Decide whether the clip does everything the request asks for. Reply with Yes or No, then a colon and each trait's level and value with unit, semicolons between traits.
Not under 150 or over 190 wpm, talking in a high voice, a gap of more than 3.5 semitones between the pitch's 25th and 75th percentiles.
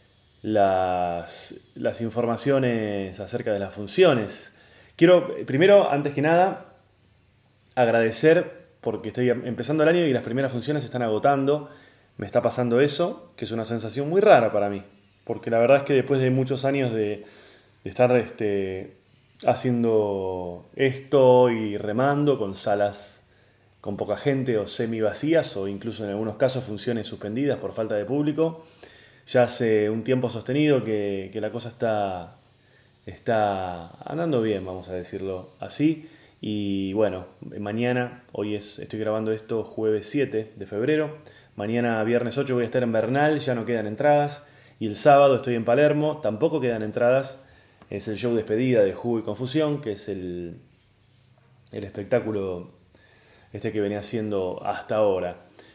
No: average, 155 wpm; low, 115 Hz; average, 4.4 semitones